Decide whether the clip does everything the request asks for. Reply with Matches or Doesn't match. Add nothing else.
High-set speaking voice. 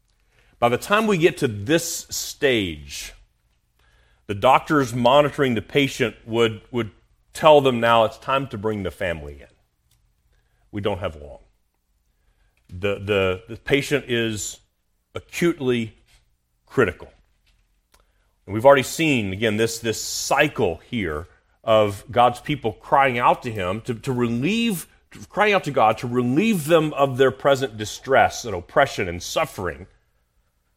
Doesn't match